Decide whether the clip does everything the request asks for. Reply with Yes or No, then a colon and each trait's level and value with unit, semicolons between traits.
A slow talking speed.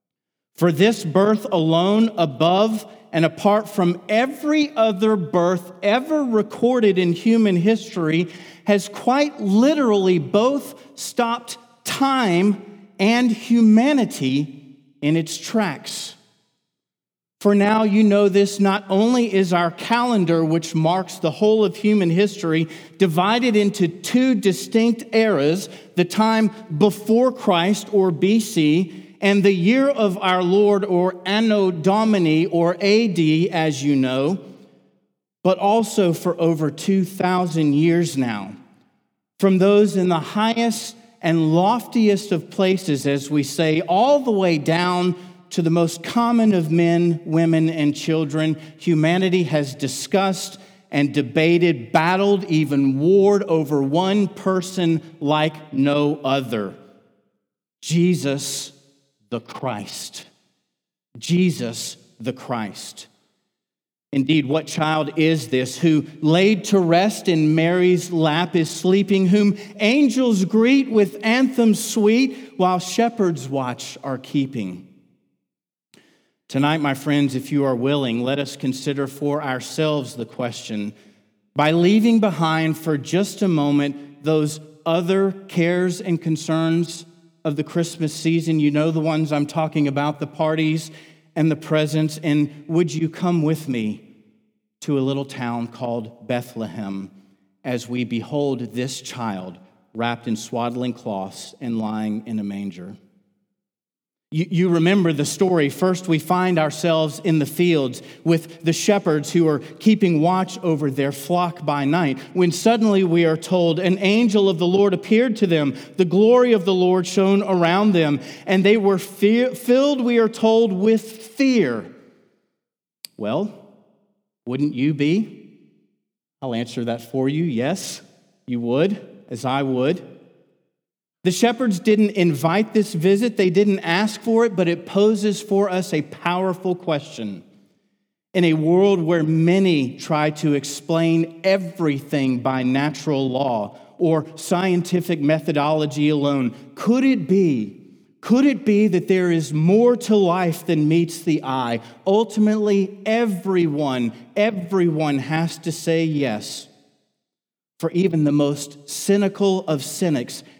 Yes: slow, 130 wpm